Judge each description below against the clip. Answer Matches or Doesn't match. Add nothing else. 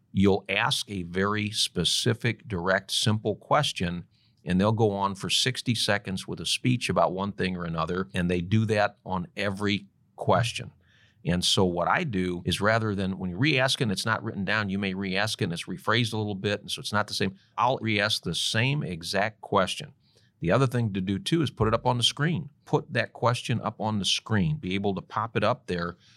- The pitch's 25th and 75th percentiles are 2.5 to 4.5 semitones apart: Matches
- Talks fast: Matches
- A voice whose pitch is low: Matches